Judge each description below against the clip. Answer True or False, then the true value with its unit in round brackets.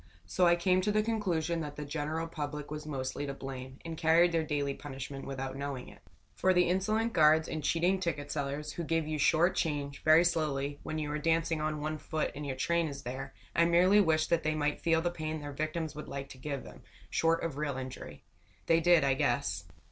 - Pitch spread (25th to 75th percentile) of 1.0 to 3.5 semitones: True (2.8 semitones)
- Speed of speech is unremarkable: False (220 wpm)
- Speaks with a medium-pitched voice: True (155 Hz)